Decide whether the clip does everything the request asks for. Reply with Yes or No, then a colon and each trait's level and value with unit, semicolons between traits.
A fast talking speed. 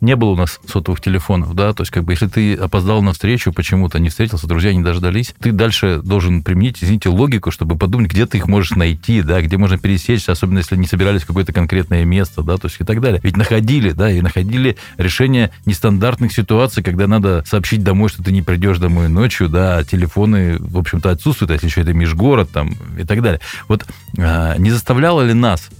Yes: fast, 210 wpm